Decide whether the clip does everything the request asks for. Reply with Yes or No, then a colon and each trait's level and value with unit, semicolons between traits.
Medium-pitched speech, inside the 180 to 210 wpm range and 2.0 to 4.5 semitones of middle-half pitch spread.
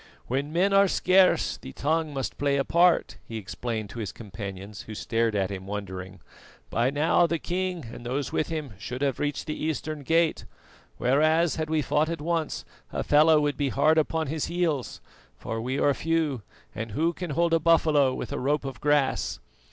No: medium, 145 Hz; average, 190 wpm; average, 5.1 semitones